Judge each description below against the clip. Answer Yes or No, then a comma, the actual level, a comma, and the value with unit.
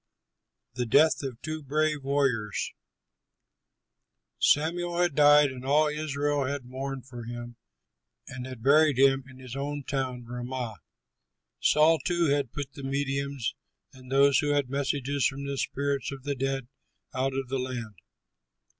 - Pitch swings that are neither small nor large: No, narrow, 2.1 semitones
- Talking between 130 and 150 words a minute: Yes, average, 145 wpm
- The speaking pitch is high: No, low, 135 Hz